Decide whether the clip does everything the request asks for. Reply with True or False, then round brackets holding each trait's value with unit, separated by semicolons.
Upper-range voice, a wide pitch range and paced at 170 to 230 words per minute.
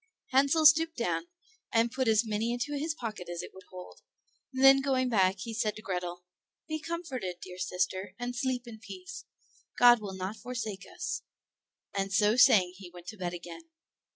True (225 Hz; 6.0 semitones; 180 wpm)